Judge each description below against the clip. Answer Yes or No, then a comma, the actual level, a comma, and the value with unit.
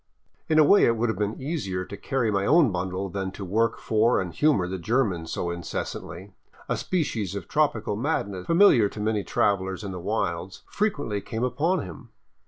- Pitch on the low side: Yes, low, 105 Hz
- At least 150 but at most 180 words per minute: No, average, 190 wpm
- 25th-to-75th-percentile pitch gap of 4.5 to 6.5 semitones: Yes, average, 5.1 semitones